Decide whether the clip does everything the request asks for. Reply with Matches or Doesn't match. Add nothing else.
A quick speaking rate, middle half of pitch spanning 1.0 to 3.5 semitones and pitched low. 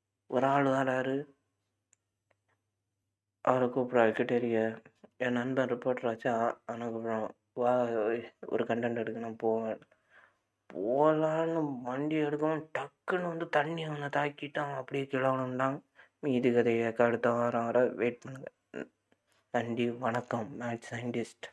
Doesn't match